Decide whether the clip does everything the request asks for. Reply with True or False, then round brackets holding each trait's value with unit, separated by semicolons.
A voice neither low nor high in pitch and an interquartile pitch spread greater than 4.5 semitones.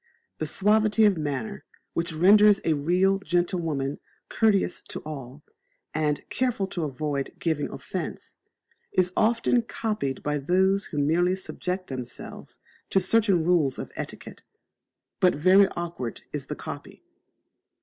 True (175 Hz; 4.9 semitones)